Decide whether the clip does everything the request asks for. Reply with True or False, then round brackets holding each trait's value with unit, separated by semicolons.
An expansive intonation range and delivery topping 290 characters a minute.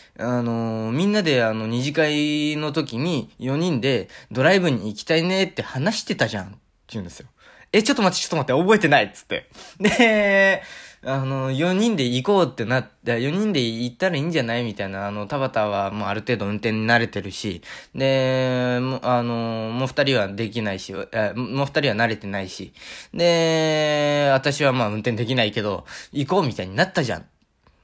True (6.1 semitones; 365 characters per minute)